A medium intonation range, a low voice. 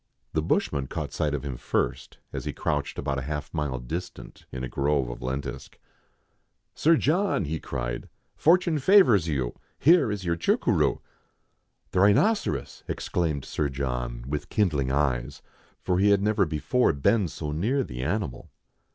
No: wide, 7.2 semitones; very low, 75 Hz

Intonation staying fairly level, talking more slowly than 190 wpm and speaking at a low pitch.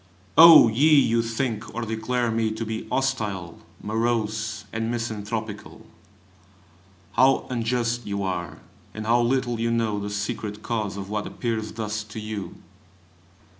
Yes: narrow, 2.0 semitones; slow, 135 wpm; low, 110 Hz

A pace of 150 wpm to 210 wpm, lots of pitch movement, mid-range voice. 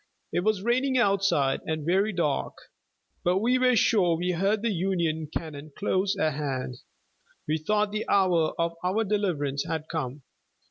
No: average, 155 wpm; average, 4.9 semitones; medium, 180 Hz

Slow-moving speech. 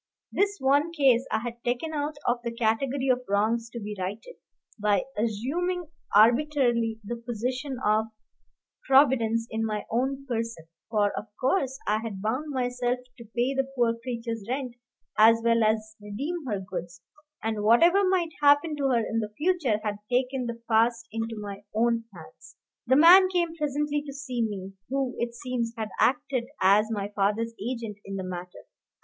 No: average, 165 wpm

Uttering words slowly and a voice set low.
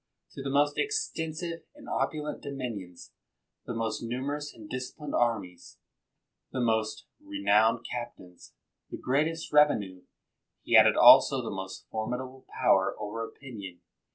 Yes: slow, 125 wpm; low, 125 Hz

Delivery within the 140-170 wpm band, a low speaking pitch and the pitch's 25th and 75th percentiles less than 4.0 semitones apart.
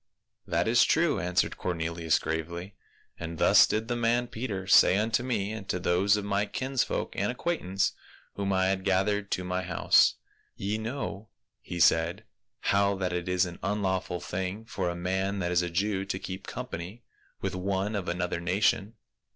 No: average, 185 wpm; very low, 95 Hz; average, 2.8 semitones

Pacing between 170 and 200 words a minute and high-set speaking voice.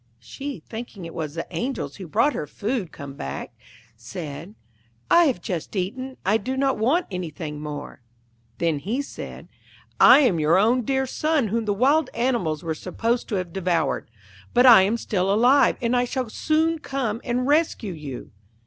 Yes: average, 175 wpm; high, 215 Hz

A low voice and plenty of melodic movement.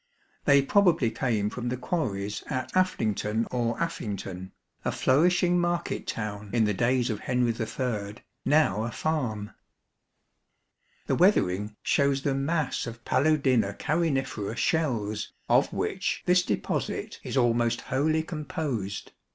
Yes: low, 125 Hz; wide, 6.2 semitones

